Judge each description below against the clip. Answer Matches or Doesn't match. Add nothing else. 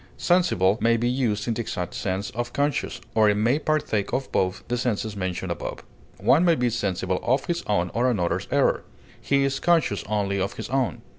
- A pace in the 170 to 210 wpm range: Matches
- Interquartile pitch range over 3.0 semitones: Matches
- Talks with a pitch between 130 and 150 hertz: Doesn't match